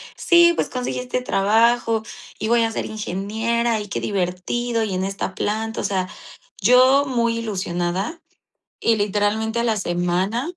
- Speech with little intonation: No, average, 3.4 semitones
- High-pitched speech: Yes, high, 220 Hz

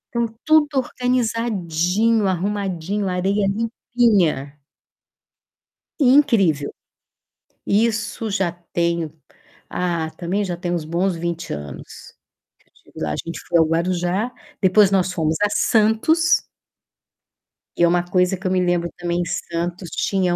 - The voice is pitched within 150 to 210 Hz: Yes, medium, 185 Hz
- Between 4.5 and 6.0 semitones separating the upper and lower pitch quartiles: No, average, 4.0 semitones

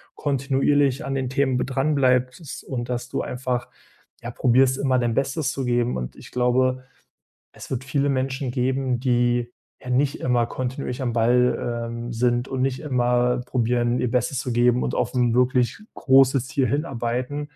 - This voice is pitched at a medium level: No, low, 125 Hz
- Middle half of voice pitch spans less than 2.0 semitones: Yes, narrow, 1.6 semitones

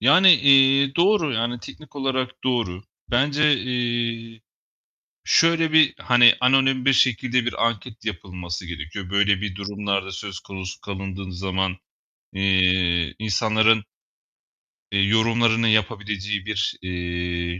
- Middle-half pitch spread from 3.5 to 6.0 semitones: Yes, average, 4.9 semitones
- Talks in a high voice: No, low, 110 Hz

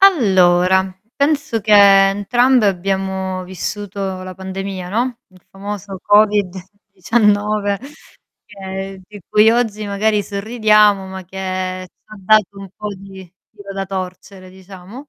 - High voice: Yes, high, 195 Hz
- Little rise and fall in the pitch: Yes, narrow, 2.0 semitones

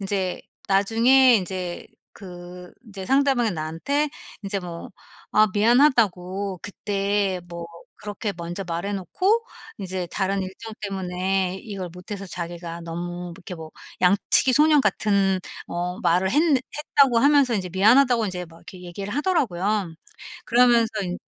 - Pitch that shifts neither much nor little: Yes, average, 4.3 semitones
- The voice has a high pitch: Yes, high, 195 Hz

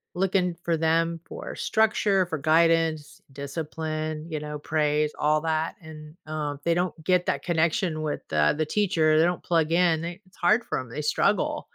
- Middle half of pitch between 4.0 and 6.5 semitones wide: No, narrow, 2.4 semitones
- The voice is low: No, medium, 160 Hz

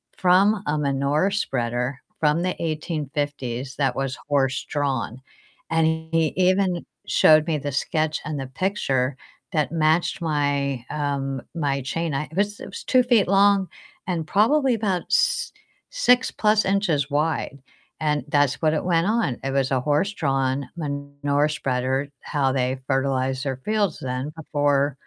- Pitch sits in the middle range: Yes, medium, 150 Hz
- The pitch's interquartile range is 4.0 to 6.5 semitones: Yes, average, 4.5 semitones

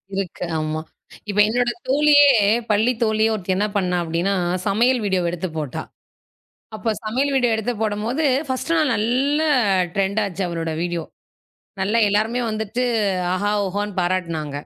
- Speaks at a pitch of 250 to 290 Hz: No, high, 205 Hz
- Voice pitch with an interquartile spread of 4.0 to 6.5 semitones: Yes, average, 4.7 semitones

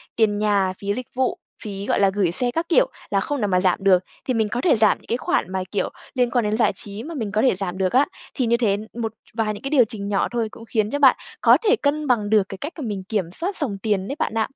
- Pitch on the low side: No, high, 220 Hz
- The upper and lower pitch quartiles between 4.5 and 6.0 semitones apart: No, average, 4.1 semitones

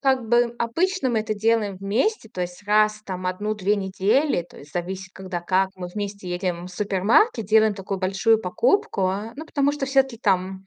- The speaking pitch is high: Yes, high, 205 Hz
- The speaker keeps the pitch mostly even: No, average, 3.8 semitones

